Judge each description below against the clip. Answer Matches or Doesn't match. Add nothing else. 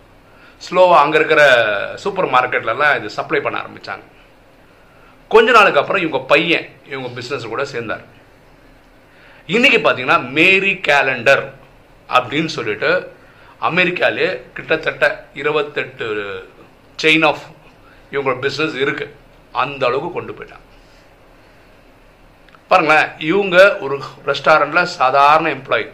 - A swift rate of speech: Doesn't match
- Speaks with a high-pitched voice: Doesn't match